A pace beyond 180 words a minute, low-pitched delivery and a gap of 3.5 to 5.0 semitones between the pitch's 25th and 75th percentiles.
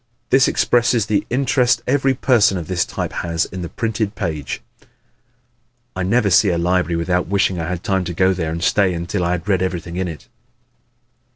Yes: average, 190 wpm; very low, 95 Hz; average, 3.8 semitones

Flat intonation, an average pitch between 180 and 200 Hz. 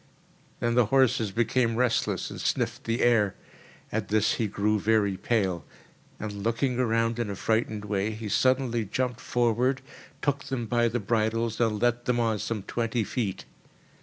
No: narrow, 2.2 semitones; low, 115 Hz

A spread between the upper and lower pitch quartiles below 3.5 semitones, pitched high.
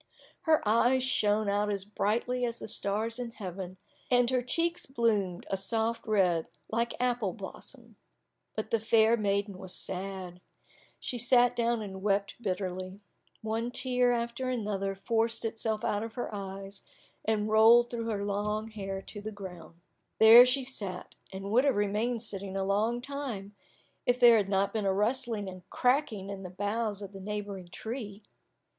Yes: average, 3.1 semitones; high, 215 Hz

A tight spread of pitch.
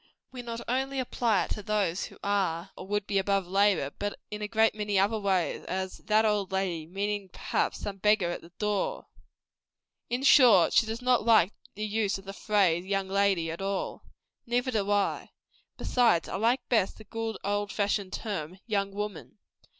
Yes: narrow, 2.3 semitones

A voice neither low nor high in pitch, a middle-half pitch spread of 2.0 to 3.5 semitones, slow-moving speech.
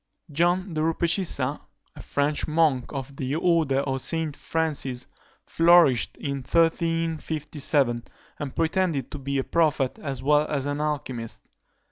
Yes: medium, 150 Hz; average, 3.2 semitones; slow, 130 wpm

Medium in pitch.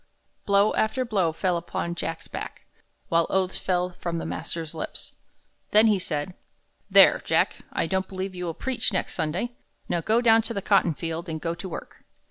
Yes: medium, 180 Hz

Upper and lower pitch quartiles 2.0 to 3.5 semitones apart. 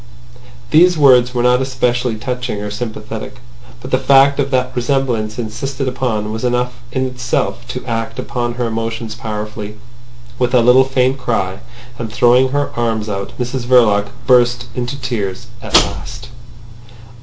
Yes: narrow, 2.4 semitones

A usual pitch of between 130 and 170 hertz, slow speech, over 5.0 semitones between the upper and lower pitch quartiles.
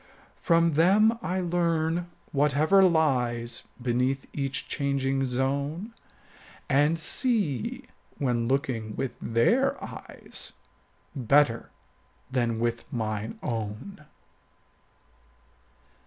Yes: medium, 140 Hz; slow, 85 wpm; wide, 5.6 semitones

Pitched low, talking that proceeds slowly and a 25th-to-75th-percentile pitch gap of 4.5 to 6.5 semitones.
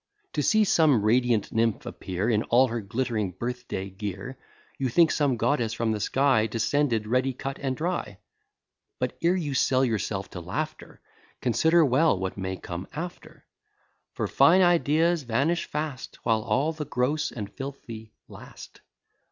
No: low, 125 Hz; average, 155 wpm; average, 5.3 semitones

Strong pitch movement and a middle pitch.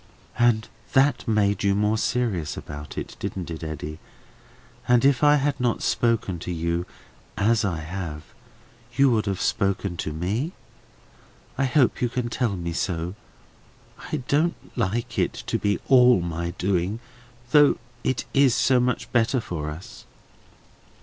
No: wide, 6.2 semitones; low, 105 Hz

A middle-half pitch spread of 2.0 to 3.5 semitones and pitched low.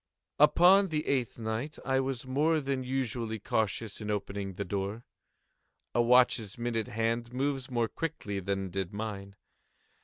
No: average, 4.5 semitones; low, 115 Hz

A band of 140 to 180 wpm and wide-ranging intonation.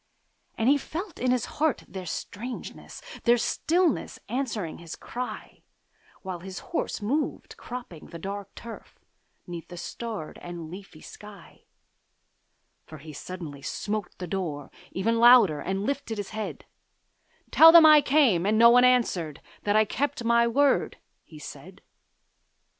Yes: average, 145 wpm; wide, 5.8 semitones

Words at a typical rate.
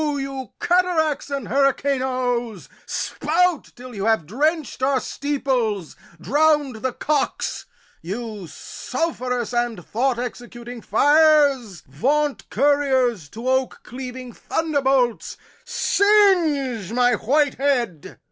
No: slow, 100 wpm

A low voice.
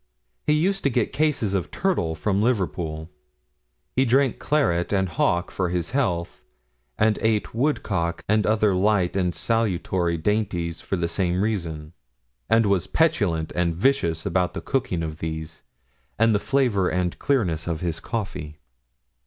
Yes: very low, 95 Hz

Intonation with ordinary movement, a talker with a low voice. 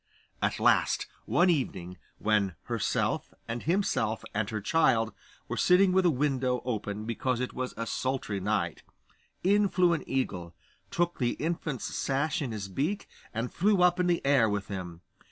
No: wide, 7.8 semitones; low, 125 Hz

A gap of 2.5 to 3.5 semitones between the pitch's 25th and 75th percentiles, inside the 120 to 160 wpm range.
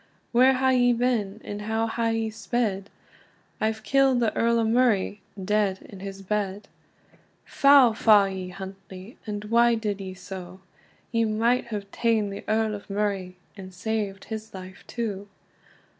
Yes: average, 2.8 semitones; average, 155 wpm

